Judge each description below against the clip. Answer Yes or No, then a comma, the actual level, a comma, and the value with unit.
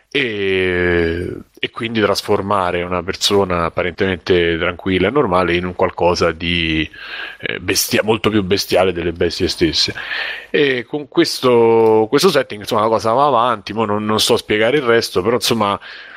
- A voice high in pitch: No, low, 100 Hz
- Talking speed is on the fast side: No, average, 150 wpm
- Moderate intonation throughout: Yes, average, 4.2 semitones